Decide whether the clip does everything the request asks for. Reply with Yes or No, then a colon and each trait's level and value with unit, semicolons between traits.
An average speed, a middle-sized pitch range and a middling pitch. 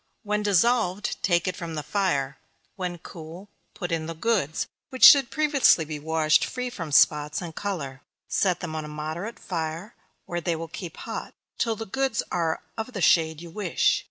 Yes: average, 185 wpm; average, 4.5 semitones; medium, 175 Hz